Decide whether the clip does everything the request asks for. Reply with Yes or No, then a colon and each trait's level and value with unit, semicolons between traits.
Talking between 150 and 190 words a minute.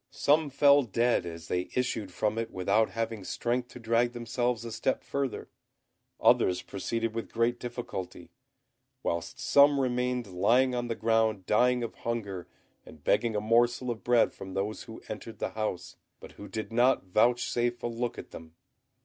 Yes: average, 165 wpm